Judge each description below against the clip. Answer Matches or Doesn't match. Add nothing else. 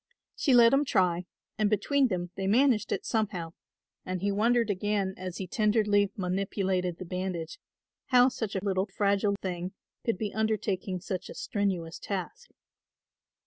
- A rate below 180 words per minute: Matches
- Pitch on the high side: Matches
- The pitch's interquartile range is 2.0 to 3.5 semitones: Matches